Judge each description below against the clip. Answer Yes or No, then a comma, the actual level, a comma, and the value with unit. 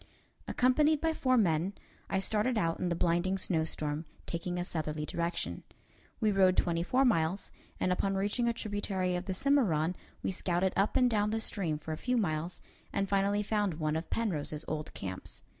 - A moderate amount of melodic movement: Yes, average, 4.3 semitones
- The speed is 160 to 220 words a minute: Yes, average, 180 wpm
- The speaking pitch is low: No, medium, 185 Hz